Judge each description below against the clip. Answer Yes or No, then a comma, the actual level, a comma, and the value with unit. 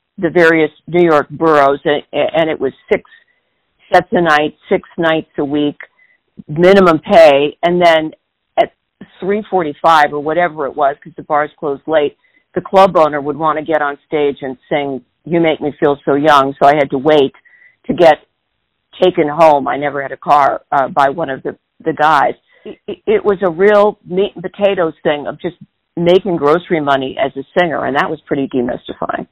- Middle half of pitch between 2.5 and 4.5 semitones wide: Yes, average, 3.9 semitones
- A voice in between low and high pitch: Yes, medium, 160 Hz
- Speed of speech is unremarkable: Yes, average, 190 wpm